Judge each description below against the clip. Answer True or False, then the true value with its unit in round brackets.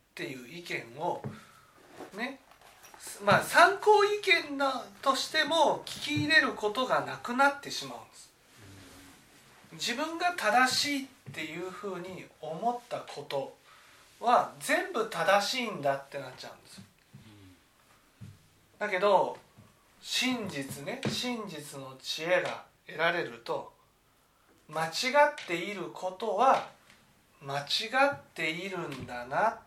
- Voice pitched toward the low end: False (200 Hz)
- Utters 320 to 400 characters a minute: False (220 characters per minute)